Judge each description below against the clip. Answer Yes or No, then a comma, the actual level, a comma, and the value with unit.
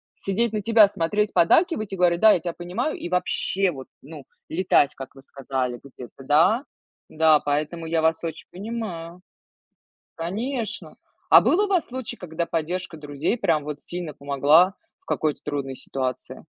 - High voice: No, medium, 170 Hz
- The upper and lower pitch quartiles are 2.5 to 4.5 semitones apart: No, wide, 5.6 semitones